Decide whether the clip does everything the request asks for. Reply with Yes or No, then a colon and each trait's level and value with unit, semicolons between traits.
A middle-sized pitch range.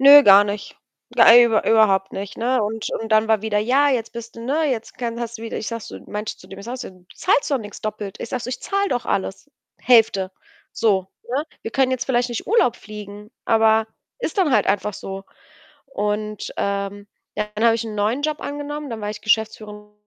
Yes: average, 3.1 semitones